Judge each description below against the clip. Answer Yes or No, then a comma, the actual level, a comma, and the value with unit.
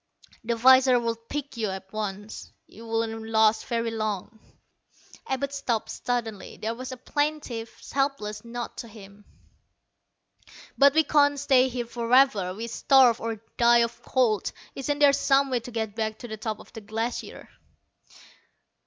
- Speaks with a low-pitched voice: No, high, 235 Hz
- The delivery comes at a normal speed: Yes, average, 155 wpm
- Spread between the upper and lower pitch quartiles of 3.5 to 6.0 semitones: No, average, 3.1 semitones